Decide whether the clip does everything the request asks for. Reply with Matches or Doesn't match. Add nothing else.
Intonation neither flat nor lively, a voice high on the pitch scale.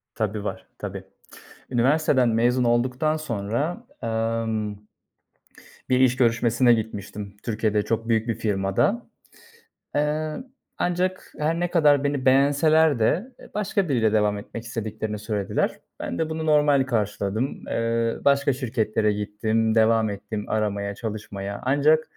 Doesn't match